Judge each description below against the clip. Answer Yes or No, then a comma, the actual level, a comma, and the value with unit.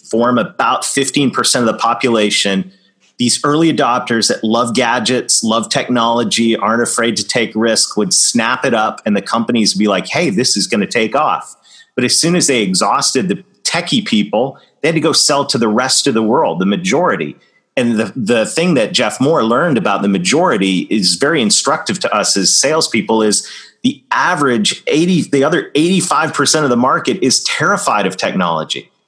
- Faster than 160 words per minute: Yes, average, 190 wpm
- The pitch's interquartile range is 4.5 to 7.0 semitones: Yes, average, 4.8 semitones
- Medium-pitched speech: No, low, 120 Hz